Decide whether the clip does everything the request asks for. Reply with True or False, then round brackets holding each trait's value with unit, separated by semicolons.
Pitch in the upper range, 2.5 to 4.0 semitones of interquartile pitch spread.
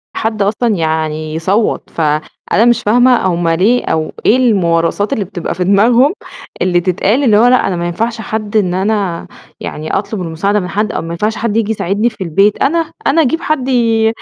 False (205 Hz; 4.9 semitones)